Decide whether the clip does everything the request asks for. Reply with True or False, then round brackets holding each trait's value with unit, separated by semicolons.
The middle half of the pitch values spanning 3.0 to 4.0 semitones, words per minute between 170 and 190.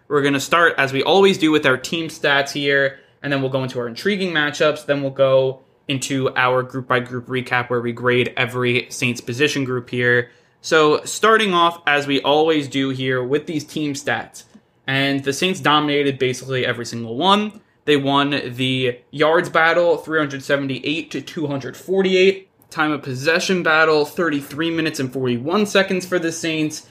True (3.7 semitones; 175 wpm)